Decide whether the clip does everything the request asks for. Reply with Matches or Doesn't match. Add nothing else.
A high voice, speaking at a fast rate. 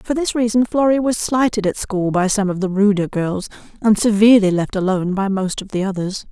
Matches